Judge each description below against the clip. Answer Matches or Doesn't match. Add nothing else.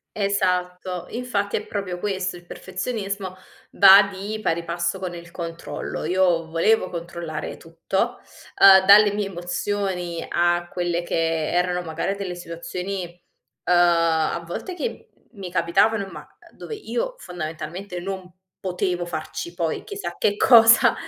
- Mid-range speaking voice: Matches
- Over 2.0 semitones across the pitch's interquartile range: Matches